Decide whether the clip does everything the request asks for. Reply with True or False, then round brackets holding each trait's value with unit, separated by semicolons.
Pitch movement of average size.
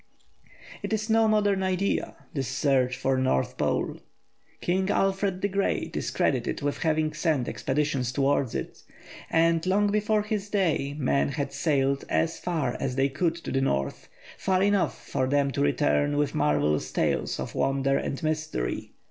False (5.7 semitones)